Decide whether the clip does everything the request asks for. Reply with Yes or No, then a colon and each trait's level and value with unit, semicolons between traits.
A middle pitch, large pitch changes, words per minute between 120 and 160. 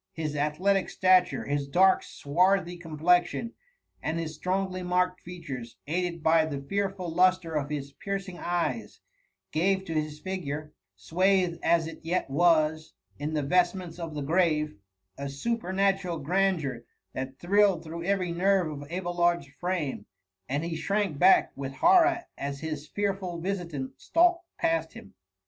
No: medium, 170 Hz; average, 3.6 semitones; average, 145 wpm